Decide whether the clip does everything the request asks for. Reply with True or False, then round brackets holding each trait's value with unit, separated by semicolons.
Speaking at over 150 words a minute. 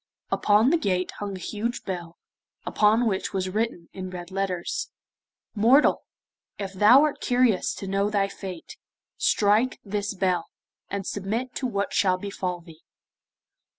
False (145 wpm)